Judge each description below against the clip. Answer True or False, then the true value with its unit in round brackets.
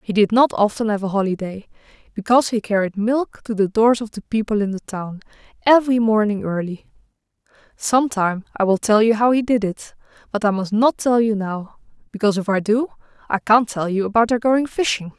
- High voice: True (215 Hz)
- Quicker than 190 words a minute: True (200 wpm)